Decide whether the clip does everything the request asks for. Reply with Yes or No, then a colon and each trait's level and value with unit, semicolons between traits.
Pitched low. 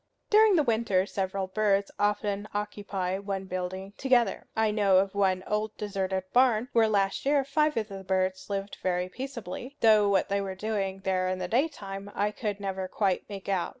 No: high, 200 Hz